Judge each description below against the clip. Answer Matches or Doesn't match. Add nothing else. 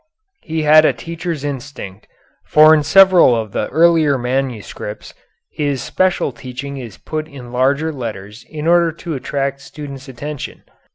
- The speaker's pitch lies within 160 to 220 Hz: Doesn't match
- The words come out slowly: Doesn't match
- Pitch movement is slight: Doesn't match